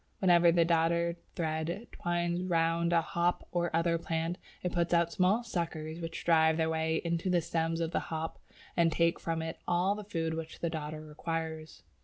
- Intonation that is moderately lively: No, narrow, 1.1 semitones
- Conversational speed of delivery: Yes, average, 185 wpm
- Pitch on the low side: No, medium, 165 Hz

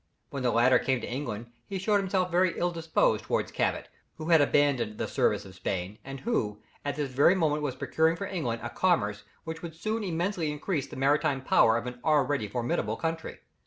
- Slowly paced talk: No, average, 200 wpm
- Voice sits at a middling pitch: Yes, medium, 145 Hz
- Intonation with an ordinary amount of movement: No, wide, 5.7 semitones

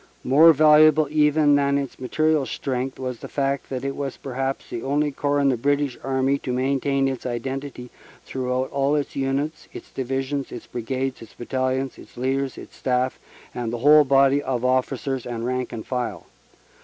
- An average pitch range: No, narrow, 1.8 semitones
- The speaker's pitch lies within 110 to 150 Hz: Yes, low, 135 Hz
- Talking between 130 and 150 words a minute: No, average, 180 wpm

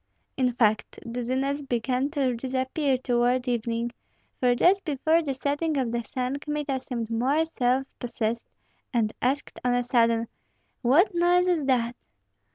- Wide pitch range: No, average, 3.1 semitones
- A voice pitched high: Yes, very high, 255 Hz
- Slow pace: No, average, 145 wpm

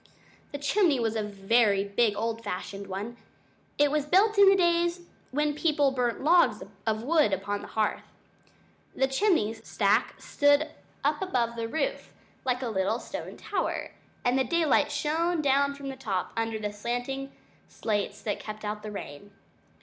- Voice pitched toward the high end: Yes, high, 245 Hz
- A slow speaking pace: No, average, 165 wpm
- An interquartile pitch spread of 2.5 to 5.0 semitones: No, wide, 5.6 semitones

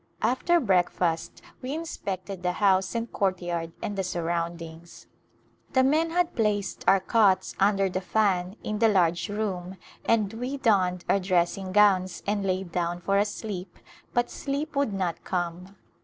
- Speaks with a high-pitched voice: Yes, high, 195 Hz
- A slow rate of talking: No, average, 155 wpm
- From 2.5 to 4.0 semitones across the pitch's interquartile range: Yes, average, 3.4 semitones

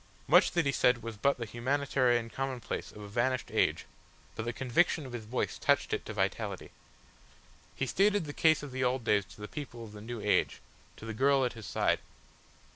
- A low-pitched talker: Yes, low, 125 Hz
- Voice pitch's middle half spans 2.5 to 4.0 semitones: Yes, average, 3.5 semitones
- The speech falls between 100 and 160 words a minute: No, fast, 205 wpm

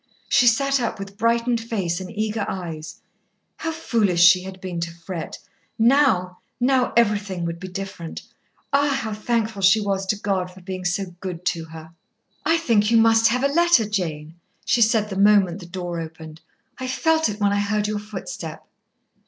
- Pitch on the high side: Yes, high, 205 Hz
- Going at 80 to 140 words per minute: No, average, 180 wpm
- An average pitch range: Yes, average, 4.3 semitones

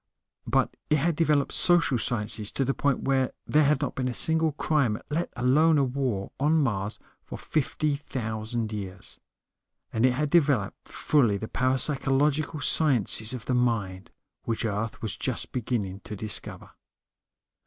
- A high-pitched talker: No, low, 130 Hz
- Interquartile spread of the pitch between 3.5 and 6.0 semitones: Yes, average, 5.1 semitones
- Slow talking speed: No, average, 155 wpm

